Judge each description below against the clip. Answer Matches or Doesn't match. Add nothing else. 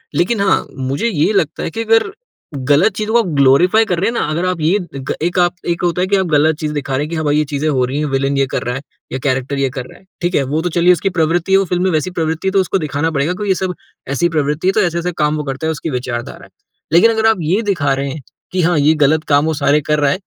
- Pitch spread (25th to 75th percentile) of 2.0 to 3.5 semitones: Doesn't match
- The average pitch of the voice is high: Doesn't match